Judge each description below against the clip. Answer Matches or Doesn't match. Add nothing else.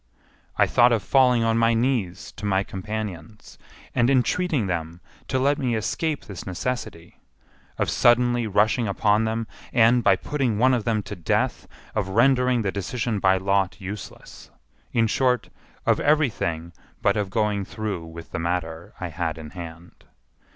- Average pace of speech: Matches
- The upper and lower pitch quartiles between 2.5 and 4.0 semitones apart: Doesn't match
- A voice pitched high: Doesn't match